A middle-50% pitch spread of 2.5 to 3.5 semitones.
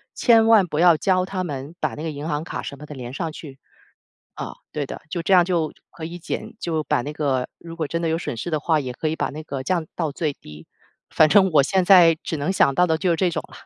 Yes: average, 3.2 semitones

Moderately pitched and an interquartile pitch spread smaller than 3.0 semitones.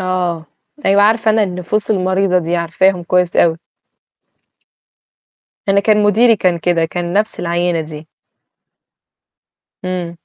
Yes: medium, 180 Hz; narrow, 2.6 semitones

